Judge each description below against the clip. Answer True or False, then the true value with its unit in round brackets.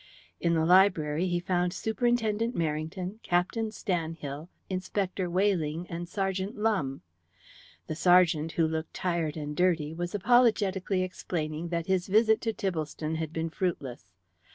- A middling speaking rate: False (130 wpm)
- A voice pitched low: False (175 Hz)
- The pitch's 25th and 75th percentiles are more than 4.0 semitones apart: False (3.2 semitones)